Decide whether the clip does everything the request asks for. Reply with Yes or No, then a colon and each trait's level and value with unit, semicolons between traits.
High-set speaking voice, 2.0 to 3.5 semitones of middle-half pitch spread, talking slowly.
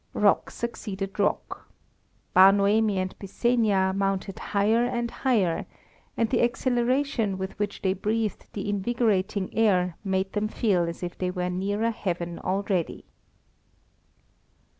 Yes: high, 200 Hz; average, 3.1 semitones; slow, 125 wpm